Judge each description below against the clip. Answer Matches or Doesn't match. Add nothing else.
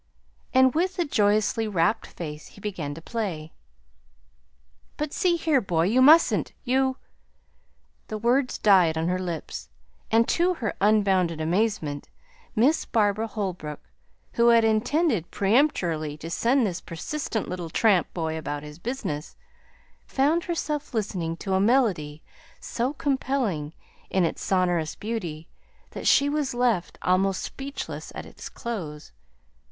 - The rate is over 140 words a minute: Doesn't match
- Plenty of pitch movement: Matches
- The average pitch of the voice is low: Doesn't match